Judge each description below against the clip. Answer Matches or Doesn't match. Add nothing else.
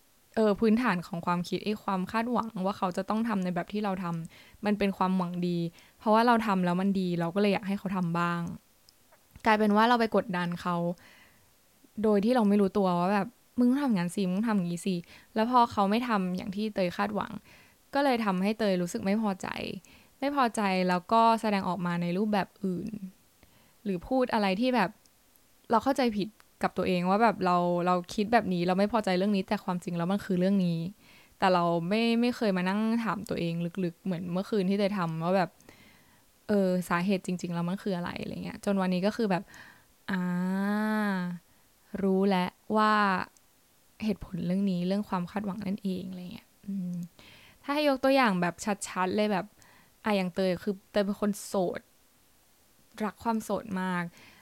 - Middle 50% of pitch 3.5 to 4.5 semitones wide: Doesn't match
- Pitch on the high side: Matches